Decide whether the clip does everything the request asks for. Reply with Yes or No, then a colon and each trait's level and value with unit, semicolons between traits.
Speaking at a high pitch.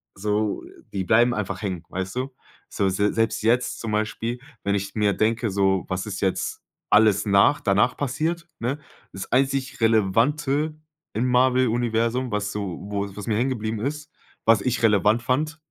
No: low, 110 Hz